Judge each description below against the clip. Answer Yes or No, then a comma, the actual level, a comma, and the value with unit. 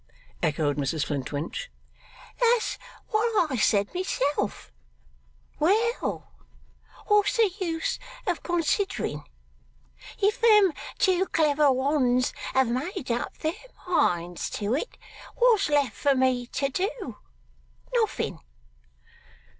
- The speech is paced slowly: Yes, slow, 100 wpm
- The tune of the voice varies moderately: No, wide, 8.4 semitones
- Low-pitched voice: No, very high, 295 Hz